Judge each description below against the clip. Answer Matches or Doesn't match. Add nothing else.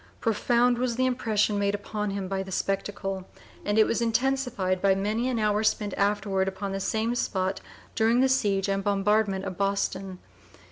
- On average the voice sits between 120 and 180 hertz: Doesn't match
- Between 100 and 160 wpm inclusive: Doesn't match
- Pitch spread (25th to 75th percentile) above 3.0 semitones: Doesn't match